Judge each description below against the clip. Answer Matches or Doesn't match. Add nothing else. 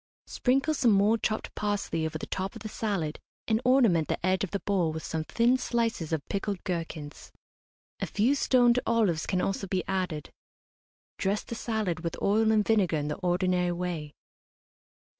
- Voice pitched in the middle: Doesn't match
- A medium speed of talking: Matches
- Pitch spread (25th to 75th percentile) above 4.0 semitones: Matches